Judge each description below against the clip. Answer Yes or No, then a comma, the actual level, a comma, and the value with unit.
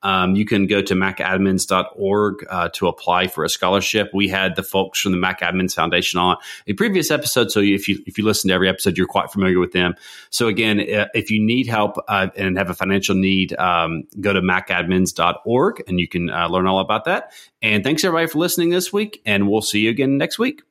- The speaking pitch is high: No, low, 100 Hz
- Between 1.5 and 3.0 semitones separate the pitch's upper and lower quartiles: Yes, average, 2.7 semitones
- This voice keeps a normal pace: No, fast, 220 wpm